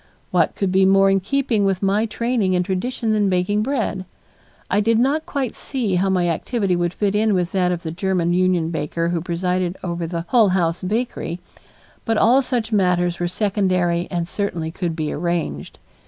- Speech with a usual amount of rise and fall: Yes, average, 3.4 semitones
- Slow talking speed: No, average, 185 wpm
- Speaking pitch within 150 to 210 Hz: Yes, medium, 185 Hz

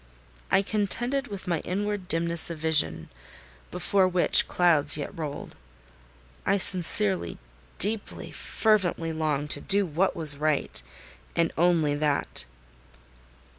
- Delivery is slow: Yes, slow, 115 wpm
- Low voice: No, medium, 170 Hz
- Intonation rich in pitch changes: No, average, 4.3 semitones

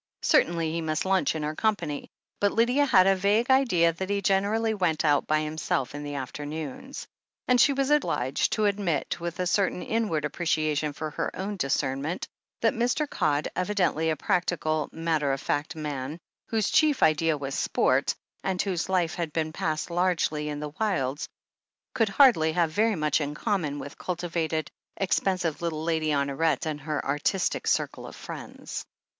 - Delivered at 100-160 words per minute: No, average, 170 wpm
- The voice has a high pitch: No, medium, 165 Hz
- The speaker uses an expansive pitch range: No, average, 4.5 semitones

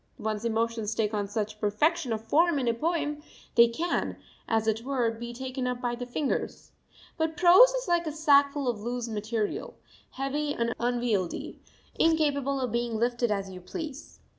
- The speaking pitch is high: Yes, high, 245 Hz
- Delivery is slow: No, average, 170 wpm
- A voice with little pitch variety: No, average, 4.7 semitones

